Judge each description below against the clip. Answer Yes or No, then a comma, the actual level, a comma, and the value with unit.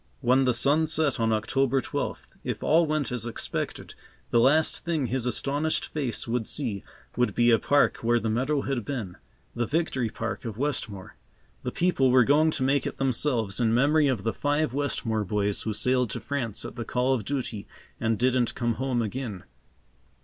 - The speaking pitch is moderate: No, low, 125 Hz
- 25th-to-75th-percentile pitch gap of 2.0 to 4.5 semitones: Yes, average, 3.8 semitones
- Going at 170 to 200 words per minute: Yes, average, 185 wpm